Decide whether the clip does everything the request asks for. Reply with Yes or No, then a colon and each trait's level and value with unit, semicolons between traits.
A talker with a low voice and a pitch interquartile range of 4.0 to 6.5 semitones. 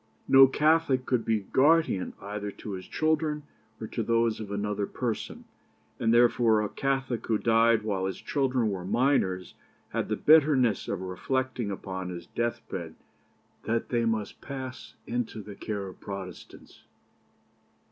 Yes: low, 115 Hz; average, 4.4 semitones